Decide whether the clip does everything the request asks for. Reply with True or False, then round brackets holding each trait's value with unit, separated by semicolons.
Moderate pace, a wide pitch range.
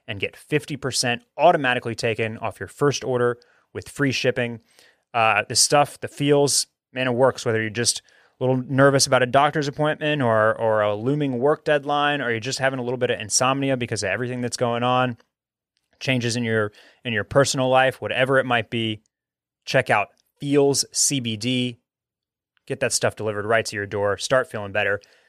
False (185 wpm; 3.3 semitones)